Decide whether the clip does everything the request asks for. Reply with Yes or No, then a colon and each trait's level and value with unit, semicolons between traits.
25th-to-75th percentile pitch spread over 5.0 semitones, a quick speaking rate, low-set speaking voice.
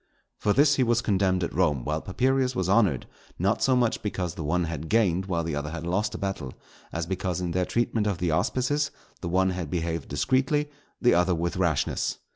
Yes: wide, 5.4 semitones; fast, 210 wpm; very low, 95 Hz